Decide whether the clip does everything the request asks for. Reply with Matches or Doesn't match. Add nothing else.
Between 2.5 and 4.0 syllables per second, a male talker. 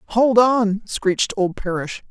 Doesn't match